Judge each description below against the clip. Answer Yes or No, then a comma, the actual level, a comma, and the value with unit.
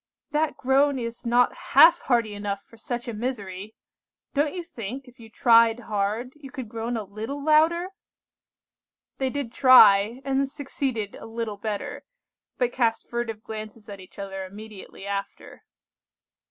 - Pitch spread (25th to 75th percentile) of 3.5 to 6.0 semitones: Yes, average, 4.1 semitones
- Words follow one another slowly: No, average, 150 wpm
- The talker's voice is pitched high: Yes, high, 230 Hz